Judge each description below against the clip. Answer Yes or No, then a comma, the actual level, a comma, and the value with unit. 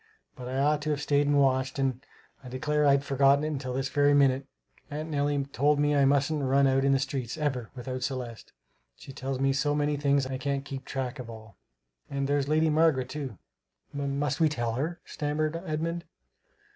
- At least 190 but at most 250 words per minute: Yes, average, 200 wpm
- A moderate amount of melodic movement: No, narrow, 1.9 semitones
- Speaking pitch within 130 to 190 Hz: Yes, medium, 140 Hz